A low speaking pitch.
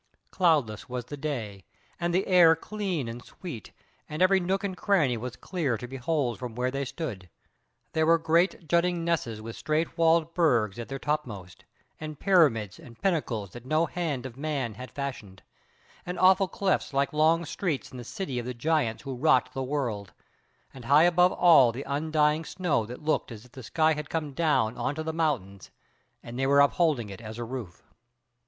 No: medium, 145 Hz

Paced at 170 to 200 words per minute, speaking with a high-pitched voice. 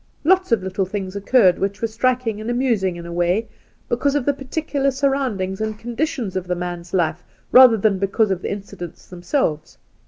Yes: average, 195 wpm; high, 210 Hz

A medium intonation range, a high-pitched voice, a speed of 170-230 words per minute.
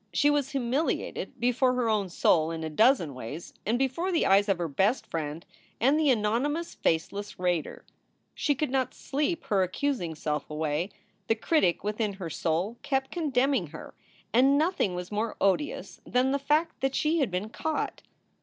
No: wide, 7.7 semitones; high, 230 Hz; average, 175 wpm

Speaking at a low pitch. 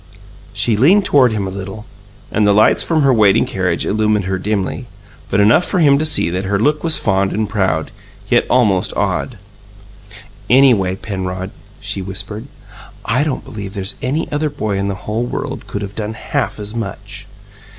Yes: low, 105 Hz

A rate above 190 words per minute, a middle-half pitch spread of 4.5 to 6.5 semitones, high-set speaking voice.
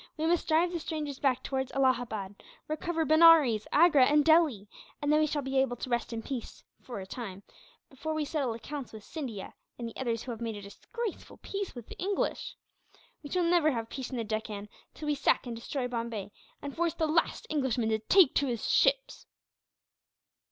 Yes: average, 200 wpm; average, 5.3 semitones; very high, 270 Hz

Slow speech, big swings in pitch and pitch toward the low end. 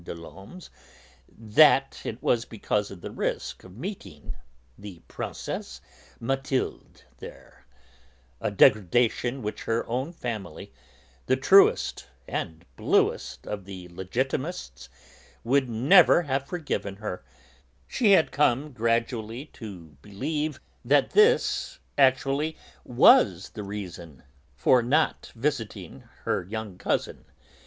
Yes: slow, 110 wpm; wide, 5.8 semitones; low, 115 Hz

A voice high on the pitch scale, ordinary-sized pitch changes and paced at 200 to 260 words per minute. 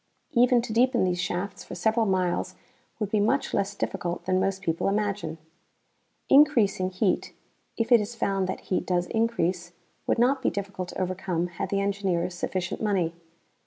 No: high, 195 Hz; average, 3.3 semitones; average, 165 wpm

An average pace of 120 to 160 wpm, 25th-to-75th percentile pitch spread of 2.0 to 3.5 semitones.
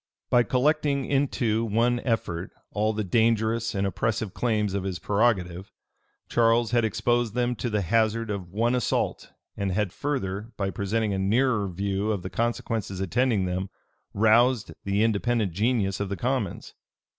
Yes: average, 155 wpm; average, 3.2 semitones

